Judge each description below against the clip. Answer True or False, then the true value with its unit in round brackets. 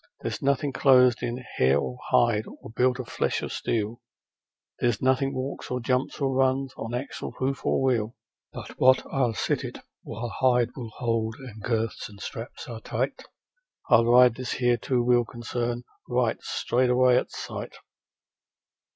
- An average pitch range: False (2.0 semitones)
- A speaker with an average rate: True (160 wpm)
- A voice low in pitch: True (125 Hz)